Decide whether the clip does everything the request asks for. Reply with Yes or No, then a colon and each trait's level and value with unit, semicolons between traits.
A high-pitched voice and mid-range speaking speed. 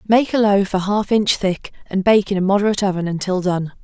No: high, 195 Hz; fast, 235 wpm